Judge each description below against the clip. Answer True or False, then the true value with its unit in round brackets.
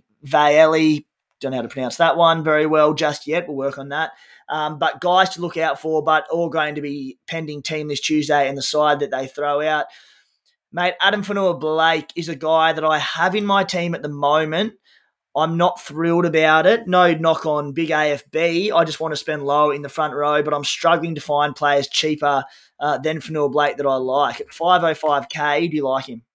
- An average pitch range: False (2.2 semitones)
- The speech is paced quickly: True (215 wpm)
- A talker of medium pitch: True (155 Hz)